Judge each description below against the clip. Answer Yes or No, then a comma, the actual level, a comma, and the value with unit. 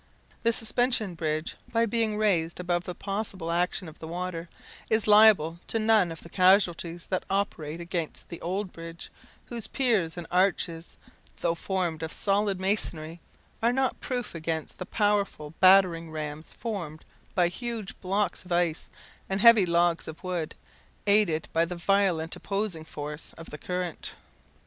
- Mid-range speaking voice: Yes, medium, 180 Hz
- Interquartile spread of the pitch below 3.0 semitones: No, average, 3.8 semitones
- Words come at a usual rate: Yes, average, 155 wpm